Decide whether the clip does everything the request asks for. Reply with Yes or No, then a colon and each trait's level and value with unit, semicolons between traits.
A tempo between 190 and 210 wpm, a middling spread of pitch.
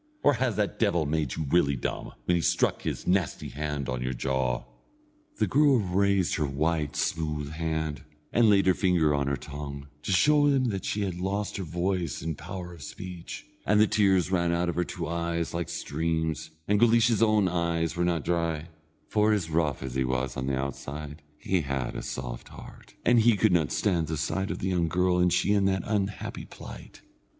Yes: average, 200 wpm; average, 4.4 semitones